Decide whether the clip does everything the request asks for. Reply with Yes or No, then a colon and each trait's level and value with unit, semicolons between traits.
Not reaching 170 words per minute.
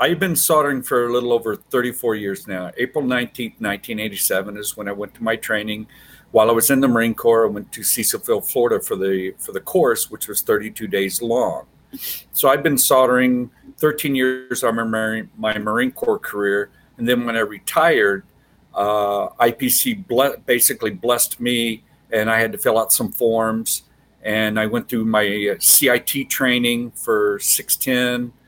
No: average, 175 wpm